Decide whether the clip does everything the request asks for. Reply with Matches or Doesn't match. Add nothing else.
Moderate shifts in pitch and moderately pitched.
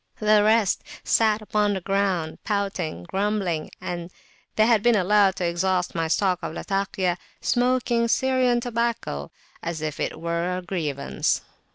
Doesn't match